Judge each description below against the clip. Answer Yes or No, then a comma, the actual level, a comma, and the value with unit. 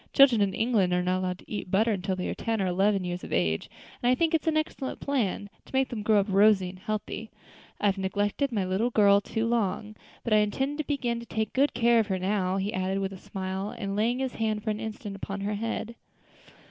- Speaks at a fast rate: Yes, fast, 245 wpm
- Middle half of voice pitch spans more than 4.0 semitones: No, average, 3.4 semitones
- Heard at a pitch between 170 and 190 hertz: No, high, 210 Hz